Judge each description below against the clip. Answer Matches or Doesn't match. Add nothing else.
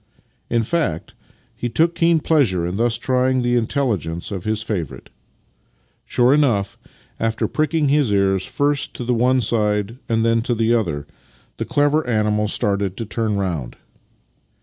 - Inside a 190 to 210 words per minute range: Doesn't match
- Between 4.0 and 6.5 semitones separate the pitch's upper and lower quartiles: Matches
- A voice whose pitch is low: Matches